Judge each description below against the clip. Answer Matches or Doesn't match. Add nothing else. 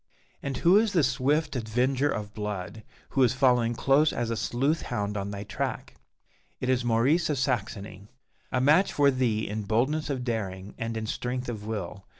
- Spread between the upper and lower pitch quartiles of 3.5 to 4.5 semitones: Matches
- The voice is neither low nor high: Doesn't match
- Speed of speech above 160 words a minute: Matches